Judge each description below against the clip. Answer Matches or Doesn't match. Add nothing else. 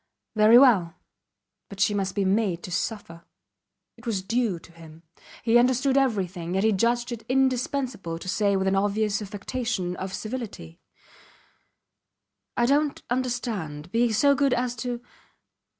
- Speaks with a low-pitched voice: Doesn't match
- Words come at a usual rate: Matches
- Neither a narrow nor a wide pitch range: Matches